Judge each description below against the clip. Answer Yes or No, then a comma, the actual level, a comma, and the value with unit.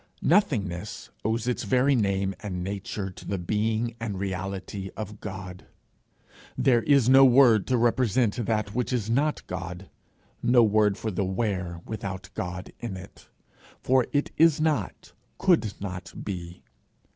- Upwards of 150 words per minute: No, average, 145 wpm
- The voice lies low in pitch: Yes, low, 105 Hz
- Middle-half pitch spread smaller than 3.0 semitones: No, average, 4.4 semitones